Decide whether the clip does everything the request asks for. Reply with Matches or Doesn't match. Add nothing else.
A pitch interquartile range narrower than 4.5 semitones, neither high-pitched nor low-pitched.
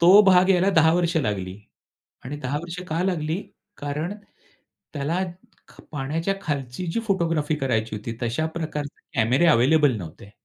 Doesn't match